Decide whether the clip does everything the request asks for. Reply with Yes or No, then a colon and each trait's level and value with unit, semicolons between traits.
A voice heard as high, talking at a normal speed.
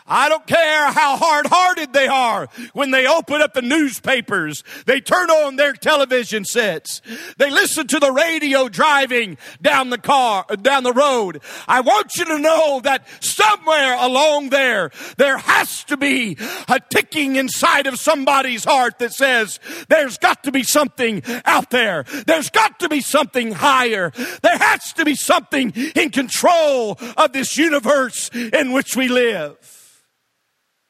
Yes: very high, 275 Hz; average, 155 wpm